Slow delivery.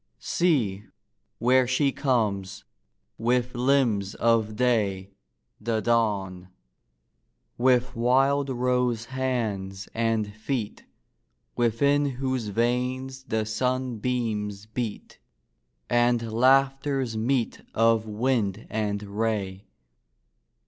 Yes: slow, 85 wpm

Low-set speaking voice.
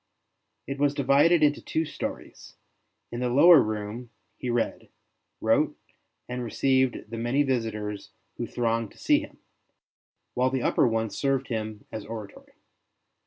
Yes: low, 120 Hz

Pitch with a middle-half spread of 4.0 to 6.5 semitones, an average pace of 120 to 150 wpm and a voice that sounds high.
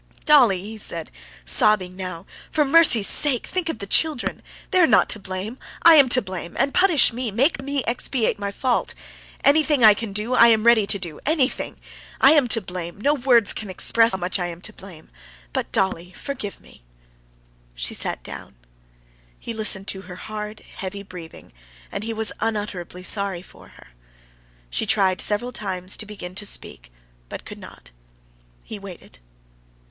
No: average, 5.0 semitones; average, 175 wpm; high, 210 Hz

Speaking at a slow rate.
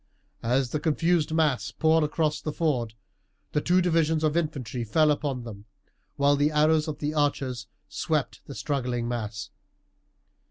No: average, 150 wpm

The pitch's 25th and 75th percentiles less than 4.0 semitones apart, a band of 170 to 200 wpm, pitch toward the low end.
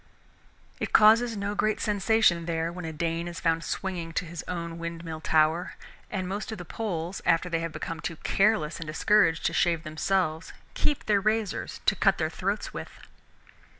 No: average, 3.5 semitones; average, 180 wpm; medium, 170 Hz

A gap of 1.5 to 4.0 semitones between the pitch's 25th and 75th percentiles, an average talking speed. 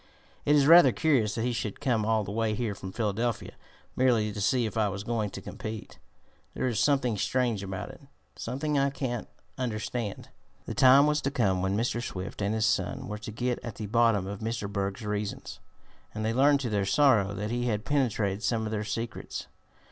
No: average, 3.2 semitones; fast, 210 wpm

